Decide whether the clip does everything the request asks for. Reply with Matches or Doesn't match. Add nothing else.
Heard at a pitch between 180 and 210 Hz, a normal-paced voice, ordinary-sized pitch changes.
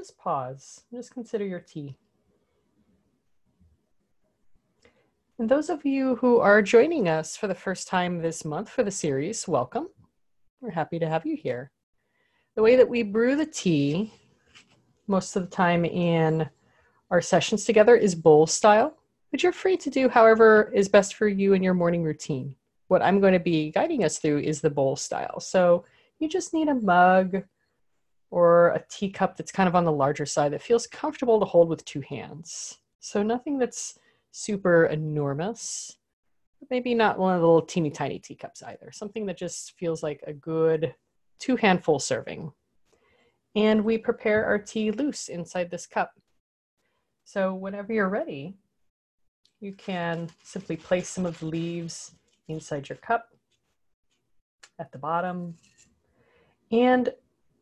Doesn't match